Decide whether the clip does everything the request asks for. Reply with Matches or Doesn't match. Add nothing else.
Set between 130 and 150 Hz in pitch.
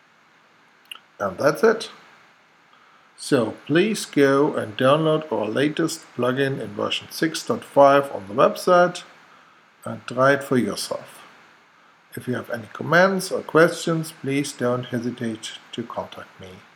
Matches